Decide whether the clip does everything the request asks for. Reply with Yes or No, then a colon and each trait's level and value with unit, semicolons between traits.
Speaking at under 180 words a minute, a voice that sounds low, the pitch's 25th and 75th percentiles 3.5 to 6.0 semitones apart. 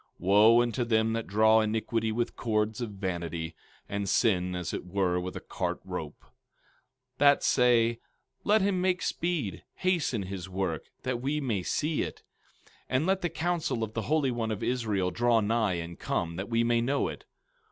No: average, 185 wpm; low, 115 Hz; average, 4.7 semitones